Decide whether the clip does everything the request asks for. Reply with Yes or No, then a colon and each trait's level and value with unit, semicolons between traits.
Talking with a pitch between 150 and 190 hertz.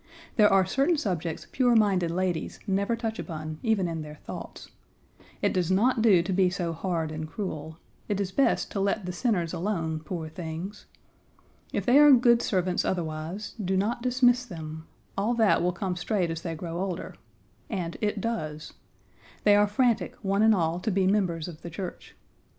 Yes: medium, 185 Hz